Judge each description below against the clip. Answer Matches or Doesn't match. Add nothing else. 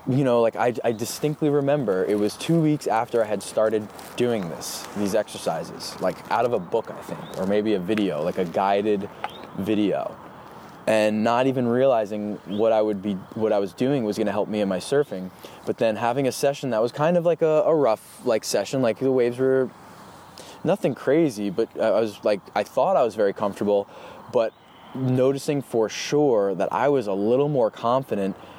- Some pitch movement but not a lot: Matches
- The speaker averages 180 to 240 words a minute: Matches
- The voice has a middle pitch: Doesn't match